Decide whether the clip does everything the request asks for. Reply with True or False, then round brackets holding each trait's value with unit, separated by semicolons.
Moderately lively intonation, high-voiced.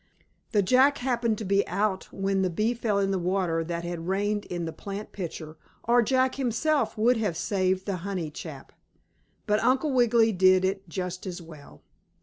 True (4.1 semitones; 195 Hz)